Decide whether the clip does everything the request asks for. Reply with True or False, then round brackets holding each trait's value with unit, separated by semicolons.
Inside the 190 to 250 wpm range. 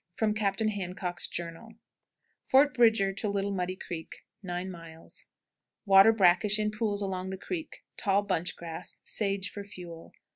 False (150 wpm)